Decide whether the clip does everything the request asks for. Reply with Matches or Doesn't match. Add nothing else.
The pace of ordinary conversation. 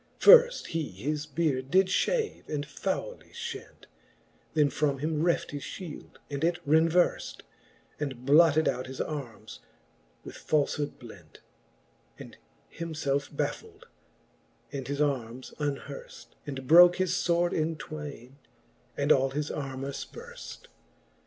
Doesn't match